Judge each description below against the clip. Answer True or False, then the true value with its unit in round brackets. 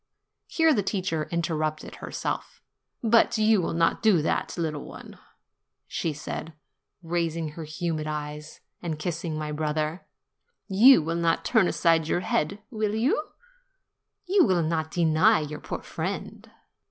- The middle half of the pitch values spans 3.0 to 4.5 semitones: True (4.0 semitones)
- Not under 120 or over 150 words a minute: True (140 wpm)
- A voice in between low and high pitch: True (165 Hz)